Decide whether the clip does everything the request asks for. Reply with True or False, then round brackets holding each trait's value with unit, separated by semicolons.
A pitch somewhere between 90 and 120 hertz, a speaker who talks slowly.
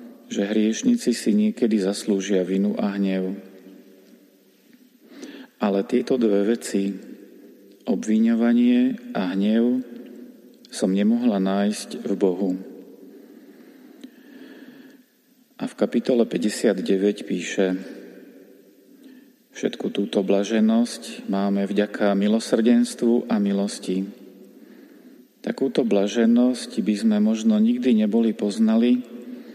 True (115 Hz; 85 wpm)